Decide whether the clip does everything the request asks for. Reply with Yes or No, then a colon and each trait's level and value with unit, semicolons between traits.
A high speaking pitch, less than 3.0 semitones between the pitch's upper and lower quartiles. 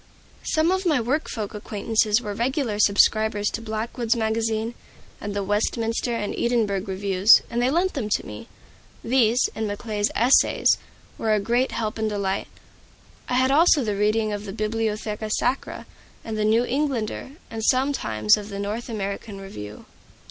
Yes: high, 220 Hz; narrow, 2.6 semitones